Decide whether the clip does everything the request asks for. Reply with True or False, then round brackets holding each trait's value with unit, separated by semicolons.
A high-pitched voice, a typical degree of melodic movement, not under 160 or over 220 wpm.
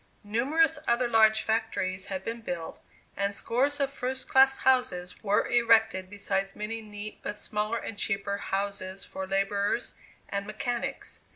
False (215 Hz; 3.0 semitones; 145 wpm)